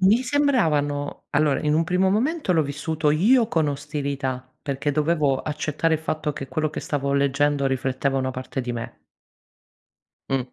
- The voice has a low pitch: No, medium, 150 Hz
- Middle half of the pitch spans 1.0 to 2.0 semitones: No, average, 2.8 semitones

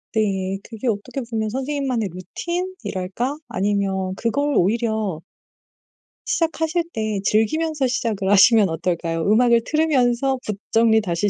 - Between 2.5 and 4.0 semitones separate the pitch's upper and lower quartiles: No, wide, 5.5 semitones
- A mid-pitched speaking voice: No, high, 225 Hz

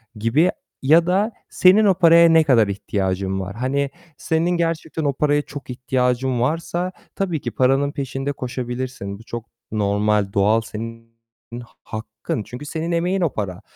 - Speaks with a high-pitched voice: No, low, 130 Hz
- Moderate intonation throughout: No, wide, 6.6 semitones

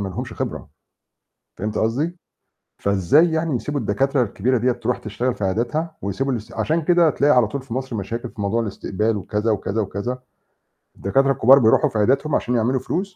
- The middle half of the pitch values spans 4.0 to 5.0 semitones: Yes, average, 4.5 semitones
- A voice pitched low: Yes, low, 120 Hz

